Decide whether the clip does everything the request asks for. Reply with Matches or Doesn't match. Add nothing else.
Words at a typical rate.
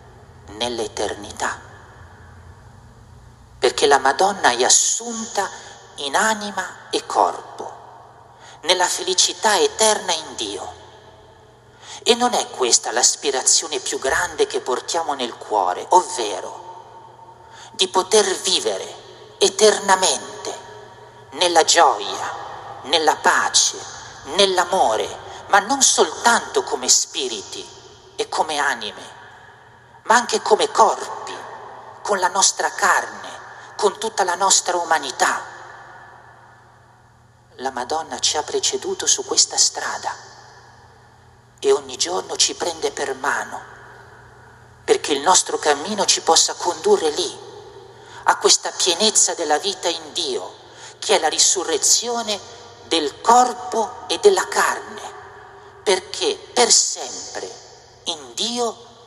Doesn't match